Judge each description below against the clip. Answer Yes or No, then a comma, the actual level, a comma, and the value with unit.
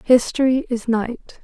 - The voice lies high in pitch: Yes, high, 245 Hz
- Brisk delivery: No, slow, 125 wpm